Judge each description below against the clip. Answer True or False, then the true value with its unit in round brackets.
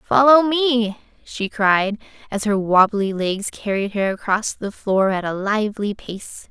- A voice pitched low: False (210 Hz)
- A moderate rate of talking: True (155 wpm)